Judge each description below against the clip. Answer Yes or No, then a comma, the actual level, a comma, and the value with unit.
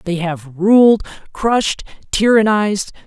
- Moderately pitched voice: No, high, 200 Hz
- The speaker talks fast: No, slow, 100 wpm